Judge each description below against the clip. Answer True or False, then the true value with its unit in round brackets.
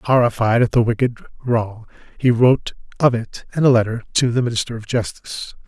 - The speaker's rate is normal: True (180 wpm)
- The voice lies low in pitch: True (120 Hz)